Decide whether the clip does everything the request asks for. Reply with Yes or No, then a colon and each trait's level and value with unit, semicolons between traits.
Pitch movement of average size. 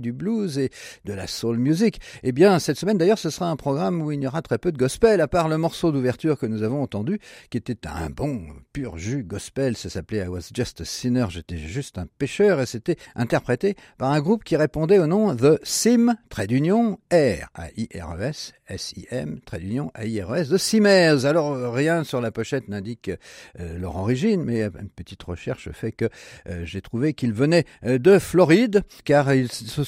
No: wide, 7.0 semitones